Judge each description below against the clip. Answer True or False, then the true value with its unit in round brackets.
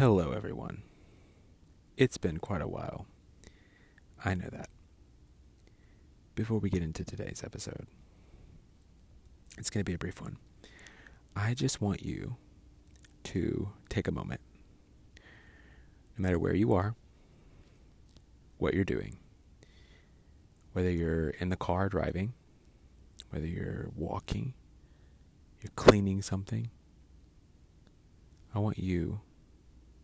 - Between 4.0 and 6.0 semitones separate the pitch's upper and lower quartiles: True (4.7 semitones)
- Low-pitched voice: True (85 Hz)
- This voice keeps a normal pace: False (110 wpm)